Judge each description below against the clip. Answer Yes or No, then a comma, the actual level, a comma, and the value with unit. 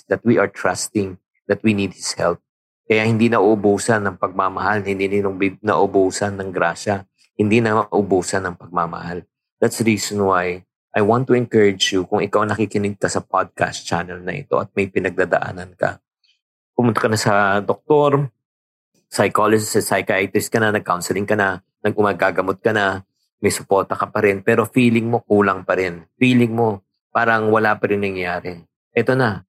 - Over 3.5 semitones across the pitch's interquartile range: No, narrow, 2.5 semitones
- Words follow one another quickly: Yes, fast, 165 wpm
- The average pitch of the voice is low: Yes, low, 100 Hz